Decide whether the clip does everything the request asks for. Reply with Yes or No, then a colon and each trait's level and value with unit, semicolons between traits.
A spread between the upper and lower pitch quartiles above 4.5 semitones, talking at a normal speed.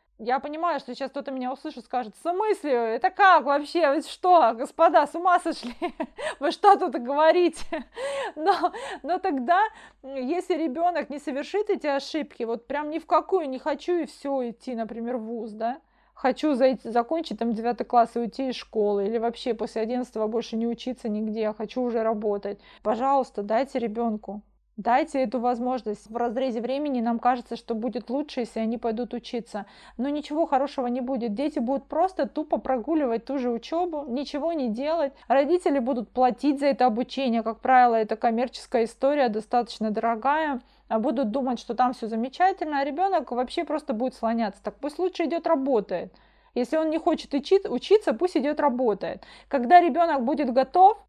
No: average, 4.9 semitones; fast, 170 wpm